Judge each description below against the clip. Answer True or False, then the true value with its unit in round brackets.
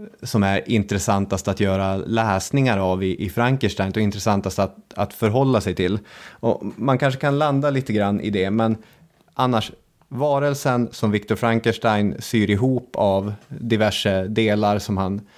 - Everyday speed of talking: True (150 wpm)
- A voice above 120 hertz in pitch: False (110 Hz)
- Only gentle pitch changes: False (3.9 semitones)